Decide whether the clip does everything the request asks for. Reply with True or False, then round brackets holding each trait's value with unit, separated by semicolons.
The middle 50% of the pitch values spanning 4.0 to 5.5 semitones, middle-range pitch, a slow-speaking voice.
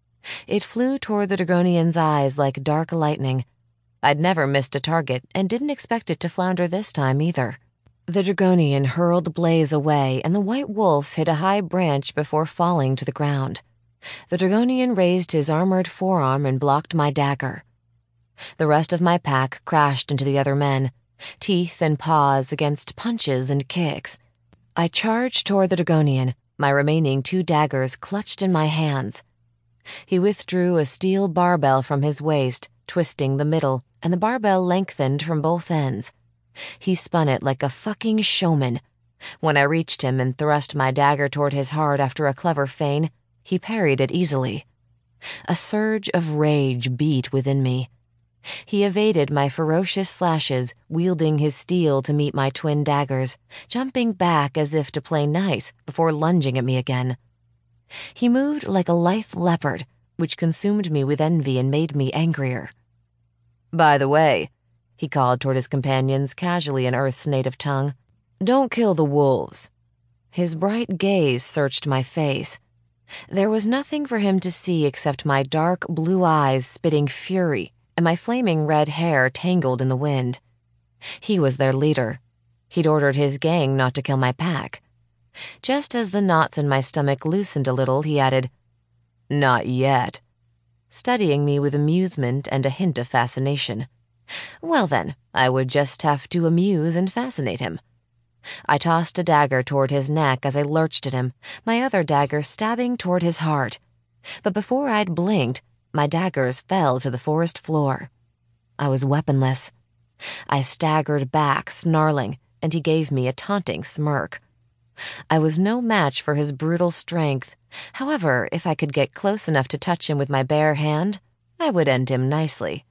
False (4.8 semitones; 145 Hz; 165 wpm)